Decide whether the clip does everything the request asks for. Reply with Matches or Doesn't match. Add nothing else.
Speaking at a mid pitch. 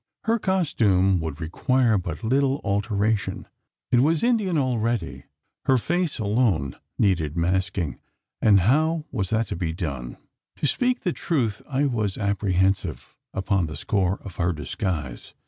Doesn't match